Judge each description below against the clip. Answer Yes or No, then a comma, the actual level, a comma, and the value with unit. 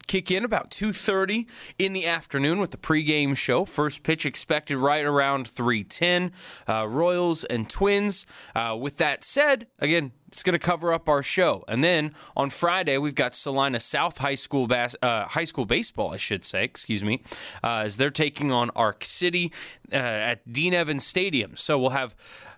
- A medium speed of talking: Yes, average, 185 wpm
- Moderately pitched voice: Yes, medium, 150 Hz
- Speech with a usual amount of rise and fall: Yes, average, 4.7 semitones